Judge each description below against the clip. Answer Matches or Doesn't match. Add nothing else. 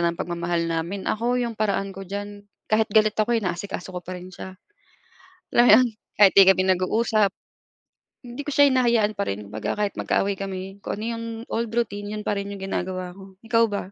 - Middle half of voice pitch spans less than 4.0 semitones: Matches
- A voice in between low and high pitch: Doesn't match